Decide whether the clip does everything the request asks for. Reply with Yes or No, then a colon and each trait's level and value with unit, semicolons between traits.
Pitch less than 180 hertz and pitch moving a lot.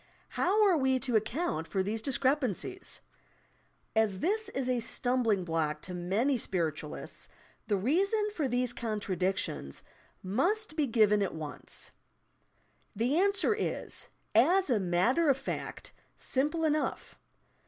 No: high, 245 Hz; wide, 8.0 semitones